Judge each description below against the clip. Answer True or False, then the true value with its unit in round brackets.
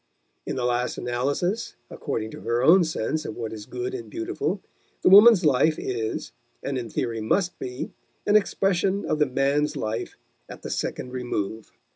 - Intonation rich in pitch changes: True (7.8 semitones)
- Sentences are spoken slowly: False (170 wpm)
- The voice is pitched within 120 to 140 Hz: True (135 Hz)